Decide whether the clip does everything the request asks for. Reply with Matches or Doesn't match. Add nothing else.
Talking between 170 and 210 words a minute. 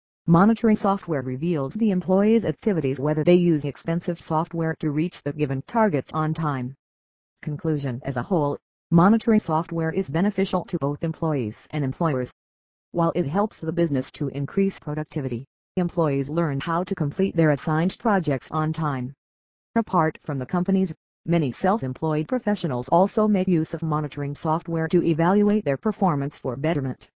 Doesn't match